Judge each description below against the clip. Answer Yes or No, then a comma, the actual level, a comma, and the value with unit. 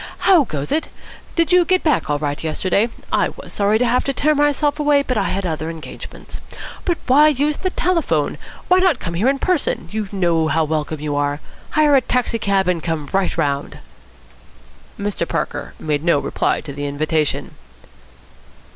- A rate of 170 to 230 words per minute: Yes, average, 180 wpm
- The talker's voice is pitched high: Yes, high, 200 Hz